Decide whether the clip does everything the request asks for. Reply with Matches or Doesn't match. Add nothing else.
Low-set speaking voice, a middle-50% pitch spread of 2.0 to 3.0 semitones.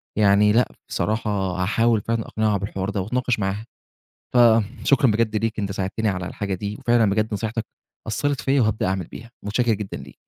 Matches